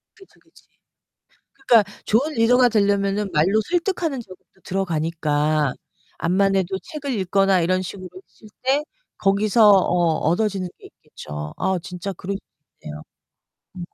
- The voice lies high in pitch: Yes, high, 195 Hz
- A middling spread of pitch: Yes, average, 3.9 semitones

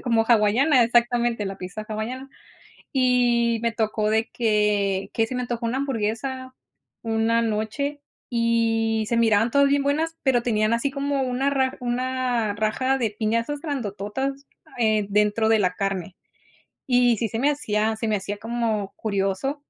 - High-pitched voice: Yes, high, 230 Hz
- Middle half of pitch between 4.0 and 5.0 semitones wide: No, average, 3.2 semitones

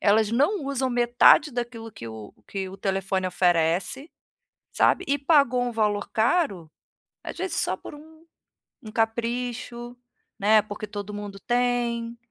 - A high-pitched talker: Yes, high, 230 Hz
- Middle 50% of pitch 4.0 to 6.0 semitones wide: No, average, 3.5 semitones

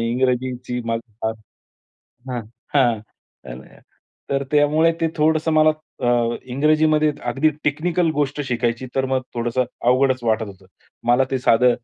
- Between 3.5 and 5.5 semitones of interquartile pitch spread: Yes, average, 4.1 semitones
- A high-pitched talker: No, low, 130 Hz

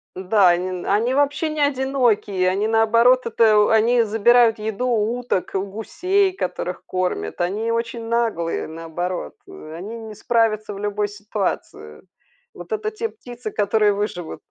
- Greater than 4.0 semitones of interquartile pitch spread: No, average, 3.6 semitones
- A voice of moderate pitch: No, high, 220 Hz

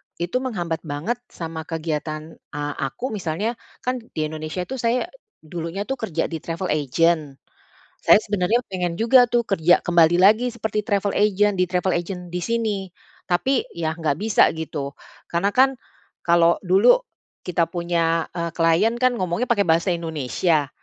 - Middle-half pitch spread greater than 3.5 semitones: Yes, average, 4.3 semitones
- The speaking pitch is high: No, medium, 175 Hz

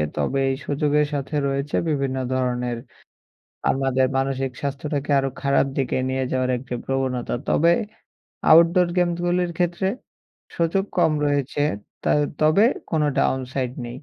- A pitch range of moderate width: Yes, average, 3.3 semitones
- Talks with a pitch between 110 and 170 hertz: Yes, medium, 140 Hz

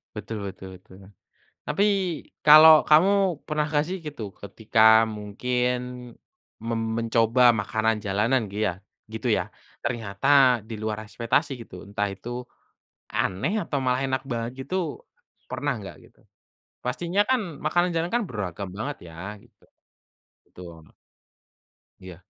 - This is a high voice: No, low, 115 Hz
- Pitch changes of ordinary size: No, wide, 6.0 semitones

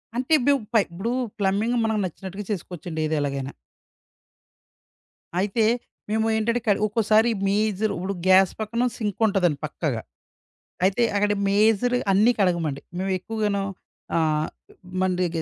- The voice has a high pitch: Yes, high, 200 Hz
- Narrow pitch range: No, average, 3.7 semitones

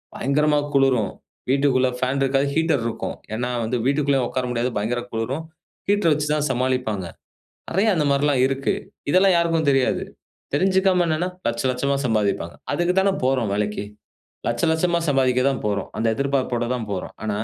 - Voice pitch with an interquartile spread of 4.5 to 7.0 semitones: No, average, 3.9 semitones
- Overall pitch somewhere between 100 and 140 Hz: Yes, low, 135 Hz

